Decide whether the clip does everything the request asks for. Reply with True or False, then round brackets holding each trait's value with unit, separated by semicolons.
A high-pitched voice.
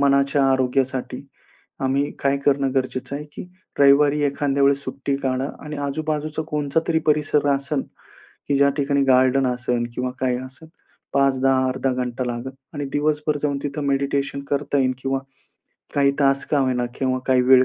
False (140 Hz)